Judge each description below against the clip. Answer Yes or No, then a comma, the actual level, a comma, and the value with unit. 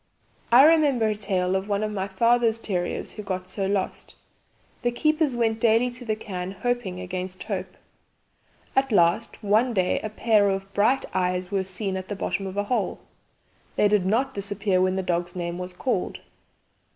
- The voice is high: Yes, high, 200 Hz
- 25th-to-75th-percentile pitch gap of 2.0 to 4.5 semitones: Yes, average, 3.7 semitones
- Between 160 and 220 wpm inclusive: Yes, average, 180 wpm